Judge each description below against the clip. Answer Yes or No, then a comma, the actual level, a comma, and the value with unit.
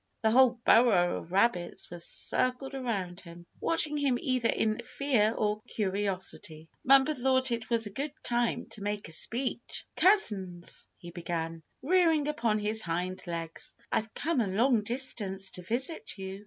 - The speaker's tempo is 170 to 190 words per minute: No, average, 155 wpm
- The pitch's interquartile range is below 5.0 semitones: No, wide, 5.6 semitones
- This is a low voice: No, high, 220 Hz